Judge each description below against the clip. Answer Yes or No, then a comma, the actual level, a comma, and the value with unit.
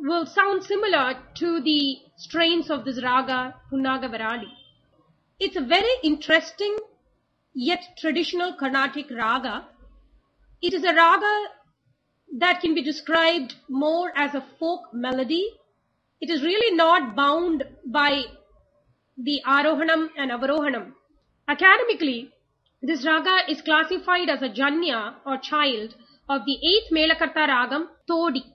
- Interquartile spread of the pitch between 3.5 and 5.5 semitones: Yes, average, 3.9 semitones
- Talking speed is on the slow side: Yes, slow, 120 wpm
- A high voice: Yes, very high, 310 Hz